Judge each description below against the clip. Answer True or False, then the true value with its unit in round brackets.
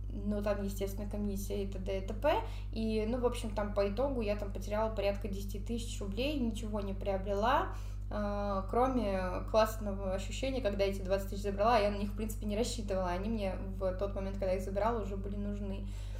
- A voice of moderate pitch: False (105 Hz)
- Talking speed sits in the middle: False (195 wpm)